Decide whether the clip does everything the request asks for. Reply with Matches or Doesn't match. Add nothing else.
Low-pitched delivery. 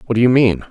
Matches